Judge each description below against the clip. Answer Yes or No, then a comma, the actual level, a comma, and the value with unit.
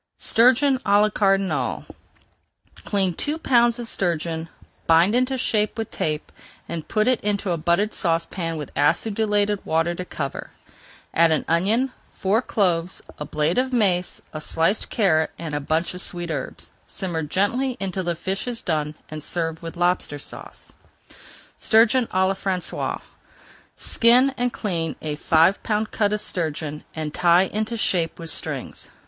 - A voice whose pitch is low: No, medium, 185 Hz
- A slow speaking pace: No, average, 155 wpm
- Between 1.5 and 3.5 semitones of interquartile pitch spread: No, average, 4.8 semitones